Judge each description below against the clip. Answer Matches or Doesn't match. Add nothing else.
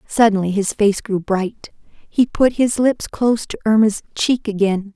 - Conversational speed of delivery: Matches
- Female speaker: Matches